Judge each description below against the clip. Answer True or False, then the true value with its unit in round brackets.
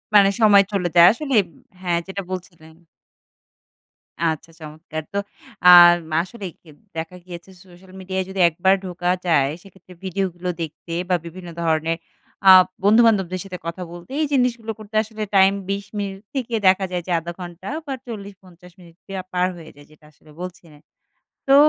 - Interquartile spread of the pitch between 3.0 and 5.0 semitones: False (2.6 semitones)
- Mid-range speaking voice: True (180 Hz)